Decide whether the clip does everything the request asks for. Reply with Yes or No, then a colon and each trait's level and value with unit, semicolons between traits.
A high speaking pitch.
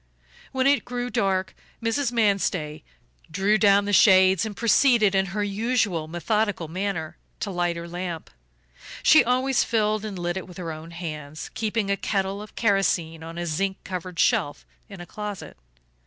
Yes: high, 195 Hz